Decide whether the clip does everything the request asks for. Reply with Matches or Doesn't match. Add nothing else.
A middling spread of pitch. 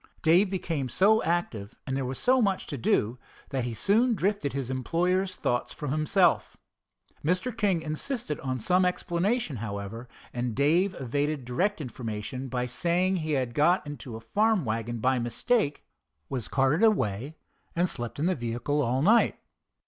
Doesn't match